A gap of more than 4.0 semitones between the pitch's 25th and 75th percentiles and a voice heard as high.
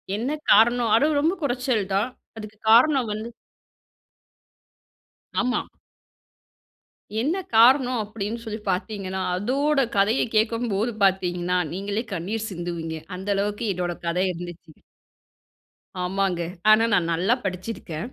Yes: average, 4.6 semitones; high, 210 Hz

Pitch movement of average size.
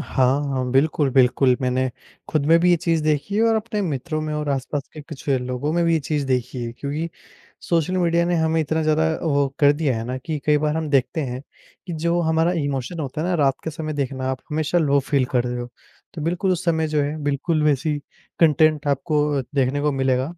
Yes: average, 3.1 semitones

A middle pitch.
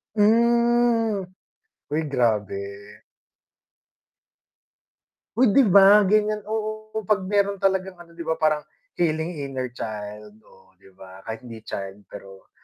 Yes: medium, 165 Hz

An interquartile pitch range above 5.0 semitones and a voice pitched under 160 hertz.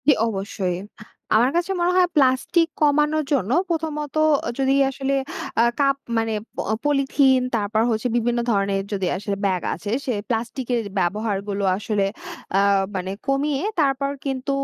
No: wide, 5.5 semitones; very high, 250 Hz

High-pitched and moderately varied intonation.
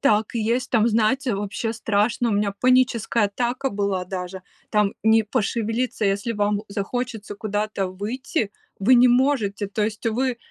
Yes: high, 220 Hz; average, 3.1 semitones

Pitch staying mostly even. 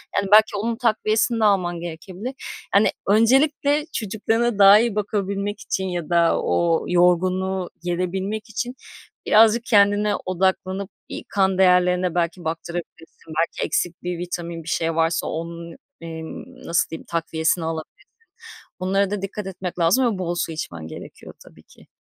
No: average, 3.4 semitones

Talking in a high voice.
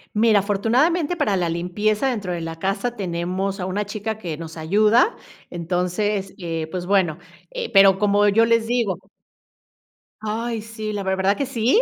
Yes: high, 205 Hz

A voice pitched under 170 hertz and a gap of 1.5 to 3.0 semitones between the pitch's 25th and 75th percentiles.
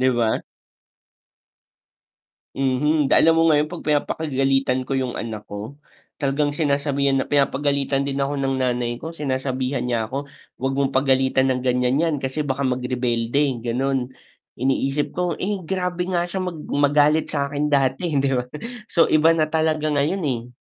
Yes: medium, 140 Hz; narrow, 2.6 semitones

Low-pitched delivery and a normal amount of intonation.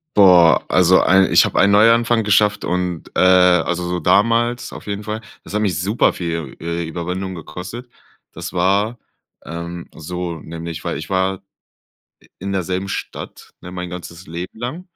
Yes: very low, 90 Hz; average, 3.0 semitones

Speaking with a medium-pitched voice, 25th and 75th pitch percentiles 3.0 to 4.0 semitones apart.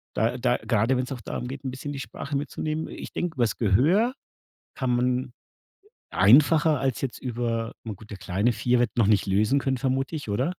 No: low, 125 Hz; average, 3.4 semitones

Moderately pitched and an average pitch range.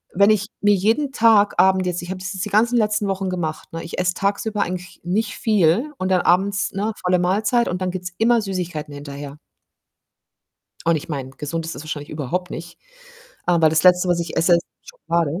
Yes: medium, 180 Hz; average, 3.6 semitones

